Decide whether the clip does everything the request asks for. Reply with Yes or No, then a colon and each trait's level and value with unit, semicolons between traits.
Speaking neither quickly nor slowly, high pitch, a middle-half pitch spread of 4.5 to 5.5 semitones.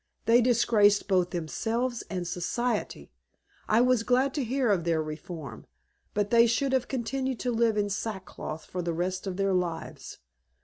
Yes: average, 165 wpm; high, 210 Hz; average, 5.1 semitones